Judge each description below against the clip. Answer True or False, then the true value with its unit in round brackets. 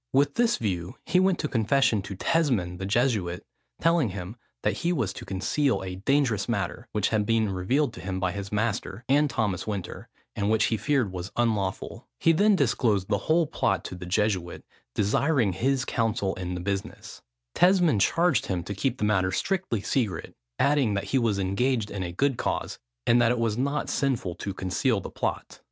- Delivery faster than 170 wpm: True (190 wpm)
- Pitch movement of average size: False (5.9 semitones)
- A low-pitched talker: True (110 Hz)